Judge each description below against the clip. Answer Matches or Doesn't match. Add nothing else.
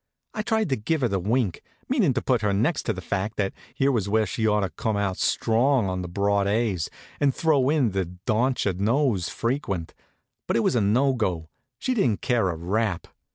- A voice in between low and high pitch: Doesn't match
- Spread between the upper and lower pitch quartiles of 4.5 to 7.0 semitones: Matches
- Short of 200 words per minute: Doesn't match